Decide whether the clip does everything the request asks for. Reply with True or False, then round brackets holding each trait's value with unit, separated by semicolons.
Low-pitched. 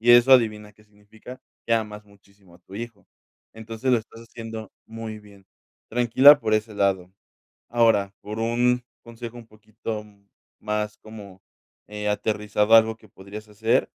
True (110 Hz)